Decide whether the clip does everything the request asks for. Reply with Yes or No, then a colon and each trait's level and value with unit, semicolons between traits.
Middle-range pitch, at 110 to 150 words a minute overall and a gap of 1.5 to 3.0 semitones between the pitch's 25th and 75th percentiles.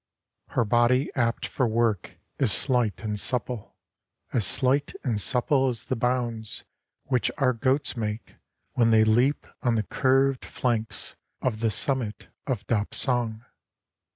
No: low, 120 Hz; slow, 135 wpm; average, 2.7 semitones